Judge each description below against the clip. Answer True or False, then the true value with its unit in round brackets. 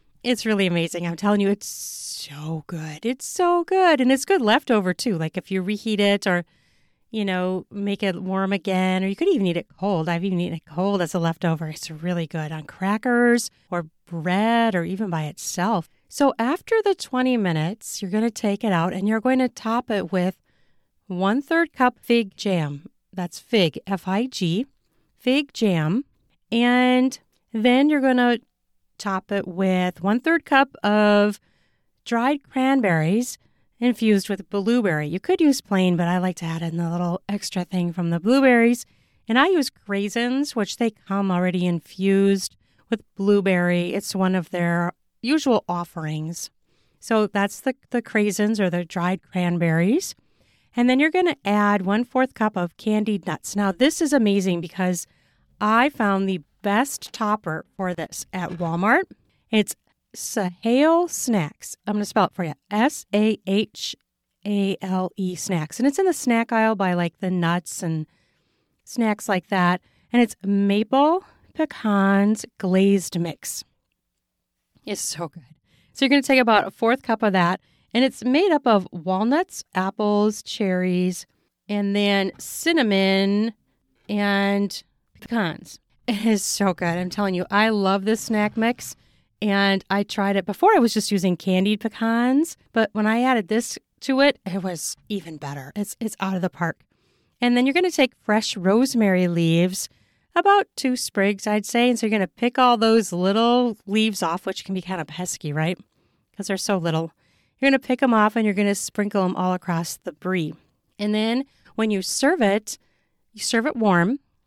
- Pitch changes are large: False (4.3 semitones)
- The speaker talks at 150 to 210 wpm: True (175 wpm)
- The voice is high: True (200 Hz)